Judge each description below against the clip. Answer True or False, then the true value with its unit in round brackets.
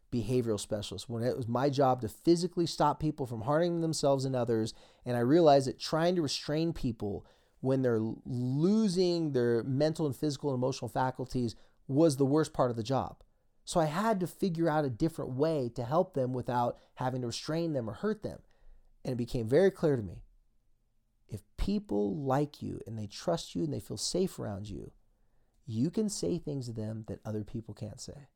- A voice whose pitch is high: False (130 Hz)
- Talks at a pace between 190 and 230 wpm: True (195 wpm)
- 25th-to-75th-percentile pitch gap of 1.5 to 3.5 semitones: False (5.1 semitones)